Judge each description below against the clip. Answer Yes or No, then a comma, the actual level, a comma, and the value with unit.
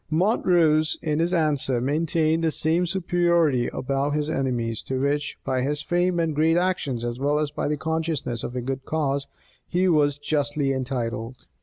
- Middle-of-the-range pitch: Yes, medium, 150 Hz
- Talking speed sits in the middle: Yes, average, 170 wpm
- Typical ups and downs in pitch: Yes, average, 3.4 semitones